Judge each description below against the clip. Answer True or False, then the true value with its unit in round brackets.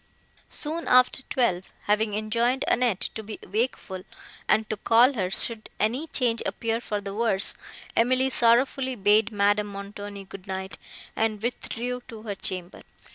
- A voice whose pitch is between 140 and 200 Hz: False (220 Hz)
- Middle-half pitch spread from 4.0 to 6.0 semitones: False (3.1 semitones)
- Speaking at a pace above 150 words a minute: False (145 wpm)